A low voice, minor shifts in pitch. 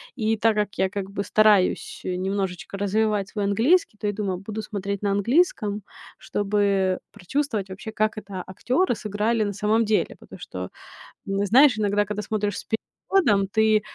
No: high, 205 Hz; narrow, 1.8 semitones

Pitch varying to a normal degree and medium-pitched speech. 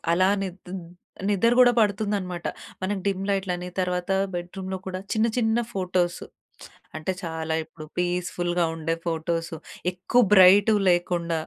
No: narrow, 2.1 semitones; medium, 180 Hz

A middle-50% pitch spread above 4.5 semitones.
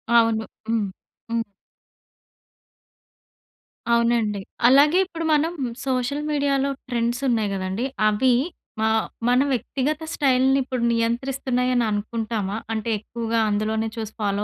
No: average, 3.3 semitones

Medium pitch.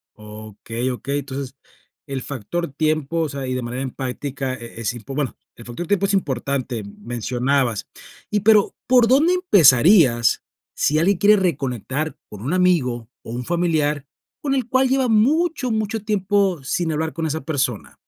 Yes: medium, 145 Hz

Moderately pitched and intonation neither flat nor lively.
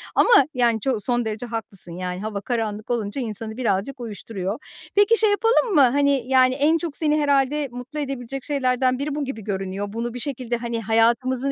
No: high, 245 Hz; average, 4.0 semitones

